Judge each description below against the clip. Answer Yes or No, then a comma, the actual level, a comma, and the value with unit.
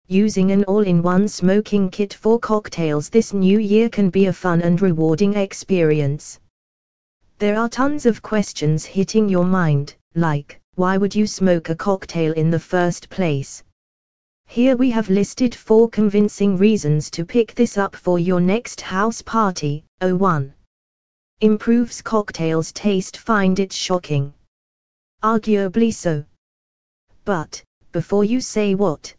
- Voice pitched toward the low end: No, high, 190 Hz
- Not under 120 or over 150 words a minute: Yes, average, 140 wpm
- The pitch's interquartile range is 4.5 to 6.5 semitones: Yes, wide, 5.5 semitones